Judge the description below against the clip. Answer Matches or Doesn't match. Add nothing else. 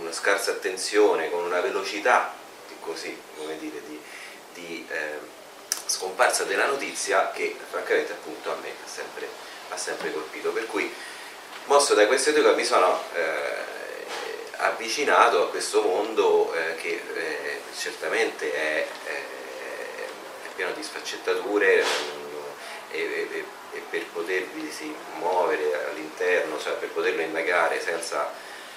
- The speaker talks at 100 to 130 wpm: Matches